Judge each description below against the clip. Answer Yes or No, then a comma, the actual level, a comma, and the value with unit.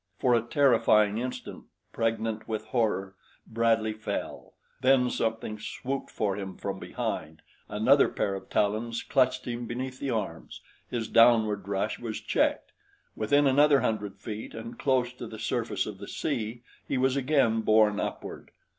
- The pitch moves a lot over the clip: No, average, 2.8 semitones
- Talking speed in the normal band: Yes, average, 150 wpm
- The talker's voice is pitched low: Yes, low, 115 Hz